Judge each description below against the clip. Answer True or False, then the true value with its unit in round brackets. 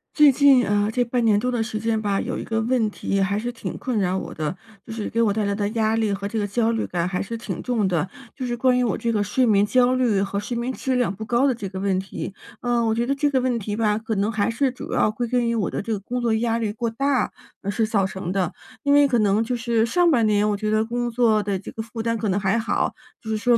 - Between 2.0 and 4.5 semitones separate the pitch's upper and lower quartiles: True (2.9 semitones)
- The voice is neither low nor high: False (225 Hz)